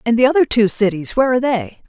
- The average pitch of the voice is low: No, high, 235 Hz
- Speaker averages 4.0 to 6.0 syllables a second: No, 6.9 syllables/s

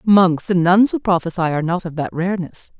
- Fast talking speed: Yes, fast, 215 wpm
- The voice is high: No, medium, 180 Hz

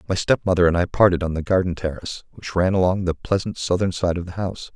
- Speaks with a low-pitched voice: Yes, very low, 90 Hz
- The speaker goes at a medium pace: No, fast, 240 wpm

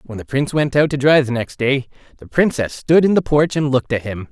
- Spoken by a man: Yes, male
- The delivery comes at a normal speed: No, fast, 265 wpm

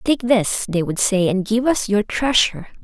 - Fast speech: Yes, fast, 210 wpm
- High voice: Yes, high, 220 Hz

